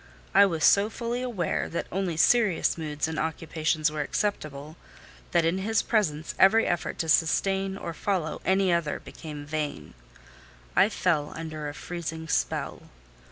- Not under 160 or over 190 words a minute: No, average, 150 wpm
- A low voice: No, medium, 165 Hz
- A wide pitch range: No, average, 3.9 semitones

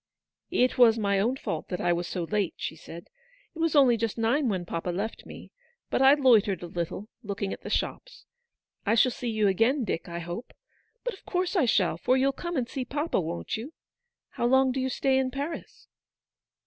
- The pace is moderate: No, fast, 215 wpm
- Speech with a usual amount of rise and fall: No, wide, 5.9 semitones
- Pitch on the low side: No, high, 230 Hz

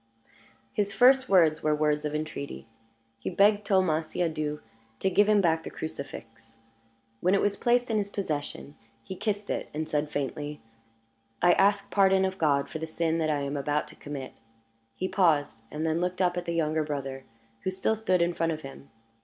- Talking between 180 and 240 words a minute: Yes, average, 190 wpm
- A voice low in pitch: No, medium, 160 Hz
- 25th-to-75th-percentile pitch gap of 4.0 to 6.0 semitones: Yes, average, 4.4 semitones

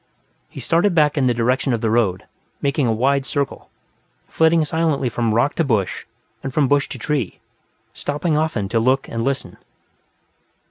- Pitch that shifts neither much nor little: Yes, average, 4.2 semitones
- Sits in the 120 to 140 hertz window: Yes, low, 135 Hz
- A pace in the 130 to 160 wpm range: No, average, 170 wpm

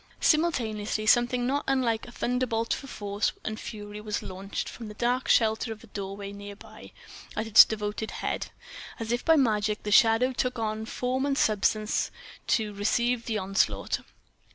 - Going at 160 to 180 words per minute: Yes, average, 170 wpm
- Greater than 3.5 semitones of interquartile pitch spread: No, average, 2.7 semitones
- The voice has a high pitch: Yes, high, 220 Hz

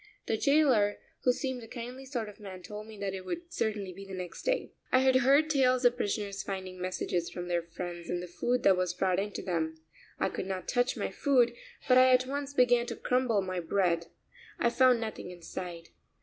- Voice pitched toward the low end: No, high, 210 Hz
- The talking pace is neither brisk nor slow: No, fast, 215 wpm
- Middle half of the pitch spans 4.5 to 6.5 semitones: Yes, wide, 5.6 semitones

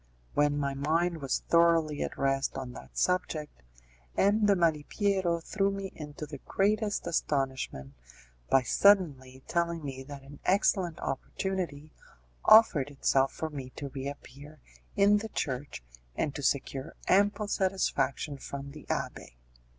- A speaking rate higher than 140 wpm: No, slow, 135 wpm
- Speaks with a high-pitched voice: No, medium, 150 Hz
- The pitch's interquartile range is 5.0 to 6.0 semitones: Yes, average, 5.3 semitones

